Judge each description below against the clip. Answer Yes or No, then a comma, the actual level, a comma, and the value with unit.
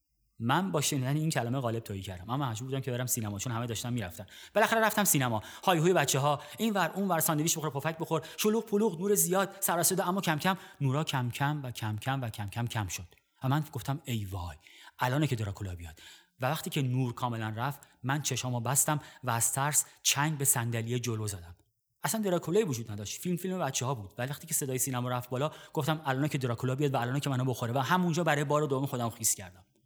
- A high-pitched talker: No, low, 135 Hz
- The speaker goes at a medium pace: No, fast, 225 wpm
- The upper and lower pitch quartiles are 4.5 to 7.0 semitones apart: Yes, average, 5.0 semitones